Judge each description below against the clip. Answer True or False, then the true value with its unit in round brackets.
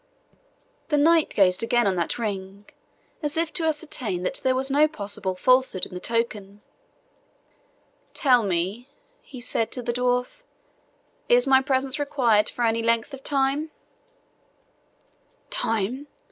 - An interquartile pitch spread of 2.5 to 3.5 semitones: False (5.2 semitones)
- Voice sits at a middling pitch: False (245 Hz)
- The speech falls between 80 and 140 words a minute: True (135 wpm)